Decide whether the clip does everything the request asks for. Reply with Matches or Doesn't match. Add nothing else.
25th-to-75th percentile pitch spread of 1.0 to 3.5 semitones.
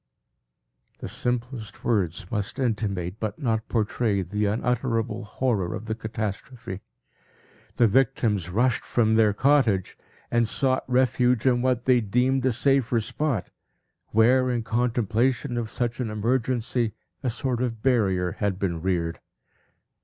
Matches